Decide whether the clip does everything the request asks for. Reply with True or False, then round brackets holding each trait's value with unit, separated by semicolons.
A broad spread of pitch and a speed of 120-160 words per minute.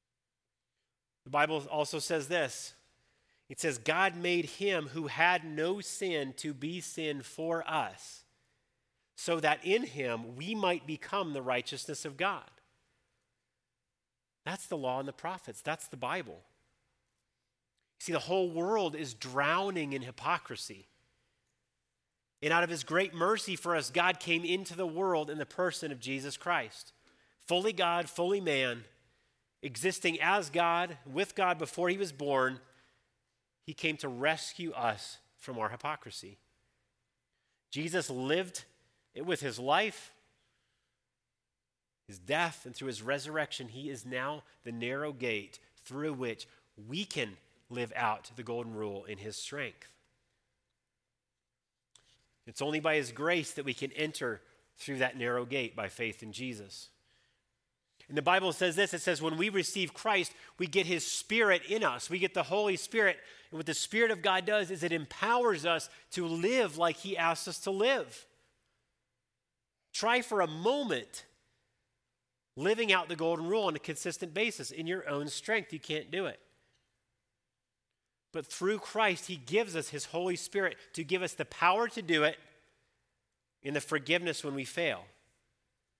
True (5.7 semitones; 155 wpm)